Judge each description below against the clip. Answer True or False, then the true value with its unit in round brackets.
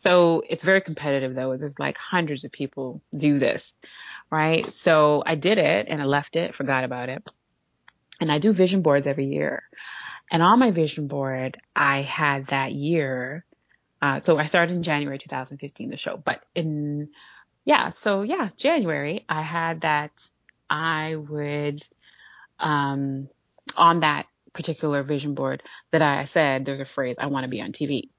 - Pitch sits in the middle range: True (150 Hz)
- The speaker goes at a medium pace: True (165 wpm)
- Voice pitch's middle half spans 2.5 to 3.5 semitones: True (3.1 semitones)